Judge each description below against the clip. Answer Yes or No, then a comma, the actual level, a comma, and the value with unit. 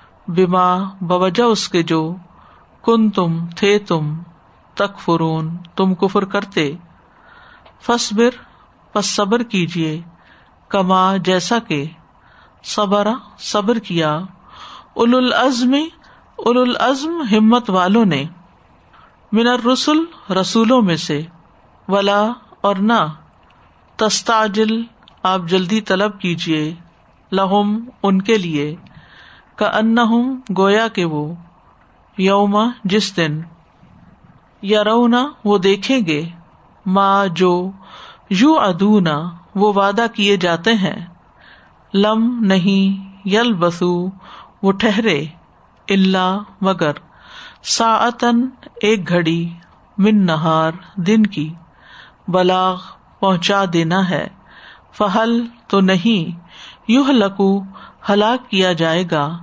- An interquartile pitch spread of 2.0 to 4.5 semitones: Yes, average, 4.2 semitones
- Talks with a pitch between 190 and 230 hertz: Yes, high, 195 Hz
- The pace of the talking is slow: Yes, slow, 100 wpm